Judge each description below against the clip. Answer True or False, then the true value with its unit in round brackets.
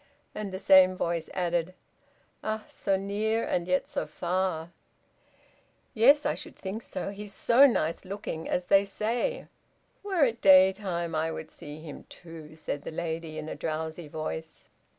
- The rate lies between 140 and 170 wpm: True (160 wpm)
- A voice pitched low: False (185 Hz)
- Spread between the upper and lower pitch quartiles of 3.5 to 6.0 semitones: True (4.2 semitones)